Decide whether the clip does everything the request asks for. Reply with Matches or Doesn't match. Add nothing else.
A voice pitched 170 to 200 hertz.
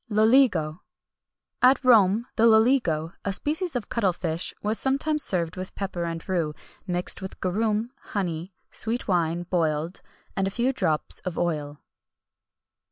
Matches